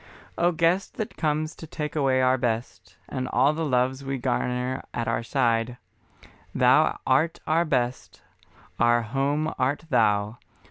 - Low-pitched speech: Yes, low, 130 Hz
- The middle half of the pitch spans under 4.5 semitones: Yes, average, 4.0 semitones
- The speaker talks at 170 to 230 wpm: No, average, 145 wpm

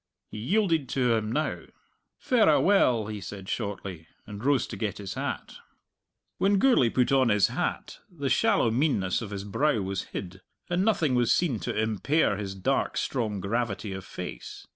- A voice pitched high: No, low, 115 Hz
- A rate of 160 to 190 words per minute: Yes, average, 170 wpm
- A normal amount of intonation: No, wide, 6.3 semitones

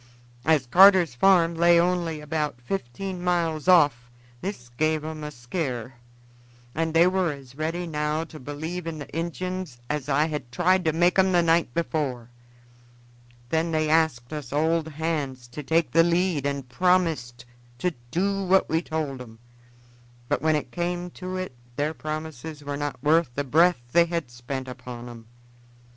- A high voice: No, medium, 155 Hz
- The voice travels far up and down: No, average, 3.7 semitones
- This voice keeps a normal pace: Yes, average, 165 wpm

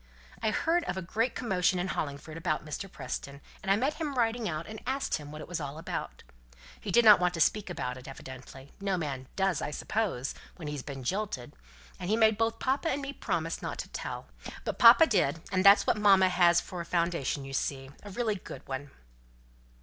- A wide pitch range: Yes, wide, 6.7 semitones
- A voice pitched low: No, medium, 180 Hz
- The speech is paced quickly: Yes, fast, 210 wpm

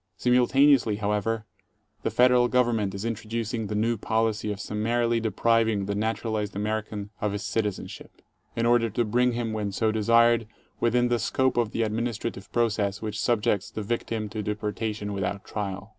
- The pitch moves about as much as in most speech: No, narrow, 2.0 semitones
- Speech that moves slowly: No, average, 165 wpm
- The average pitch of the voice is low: Yes, low, 110 Hz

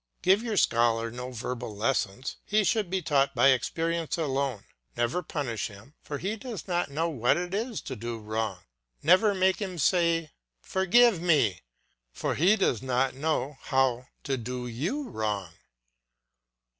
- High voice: No, medium, 140 Hz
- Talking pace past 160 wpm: No, average, 155 wpm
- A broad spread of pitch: Yes, wide, 7.1 semitones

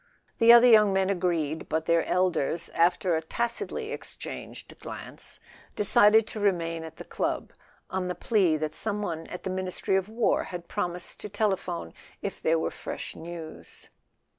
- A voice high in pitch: No, medium, 180 Hz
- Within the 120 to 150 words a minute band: No, average, 165 wpm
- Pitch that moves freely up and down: No, average, 3.9 semitones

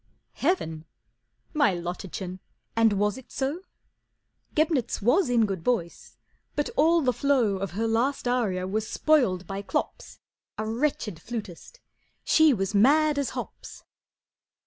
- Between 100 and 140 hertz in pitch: No, high, 225 Hz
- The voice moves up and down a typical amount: No, wide, 6.5 semitones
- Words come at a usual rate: No, slow, 130 wpm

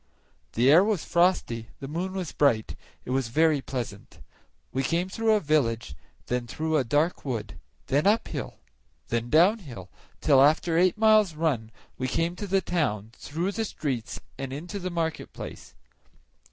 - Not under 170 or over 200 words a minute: No, average, 160 wpm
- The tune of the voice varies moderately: No, wide, 6.1 semitones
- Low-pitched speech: No, medium, 155 Hz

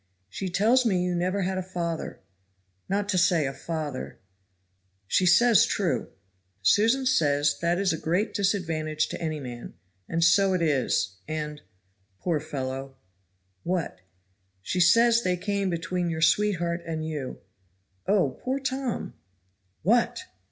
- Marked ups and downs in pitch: No, average, 4.7 semitones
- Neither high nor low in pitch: Yes, medium, 170 Hz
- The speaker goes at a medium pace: Yes, average, 145 wpm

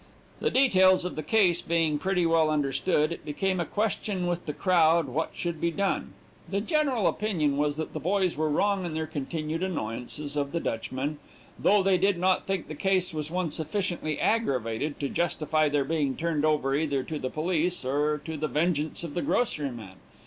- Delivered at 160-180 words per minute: No, average, 190 wpm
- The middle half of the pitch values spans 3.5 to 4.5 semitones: Yes, average, 3.8 semitones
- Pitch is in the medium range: Yes, medium, 160 Hz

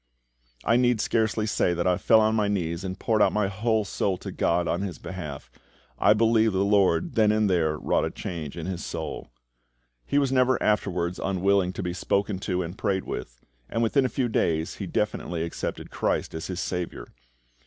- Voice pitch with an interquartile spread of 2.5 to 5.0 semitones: Yes, average, 3.9 semitones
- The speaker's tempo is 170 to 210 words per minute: Yes, average, 195 wpm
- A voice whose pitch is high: No, very low, 95 Hz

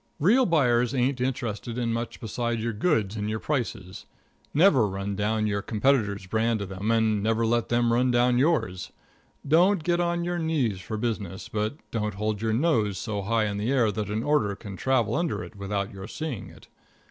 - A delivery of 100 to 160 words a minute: No, average, 195 wpm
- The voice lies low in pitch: Yes, low, 115 Hz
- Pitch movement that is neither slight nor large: Yes, average, 4.1 semitones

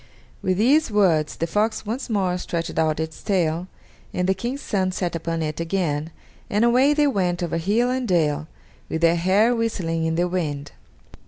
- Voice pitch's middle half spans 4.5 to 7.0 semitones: Yes, average, 4.8 semitones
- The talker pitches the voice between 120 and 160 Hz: No, medium, 180 Hz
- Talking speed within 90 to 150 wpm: No, average, 180 wpm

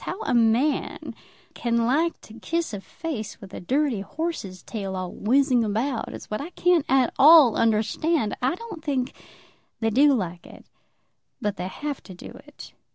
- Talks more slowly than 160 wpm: No, average, 175 wpm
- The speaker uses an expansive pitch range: Yes, wide, 5.9 semitones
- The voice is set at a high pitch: Yes, high, 245 Hz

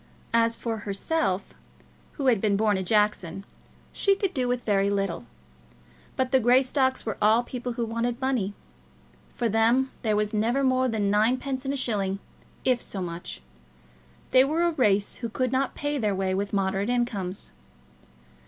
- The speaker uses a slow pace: No, average, 165 wpm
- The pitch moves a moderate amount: Yes, average, 4.3 semitones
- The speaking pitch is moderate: No, high, 230 Hz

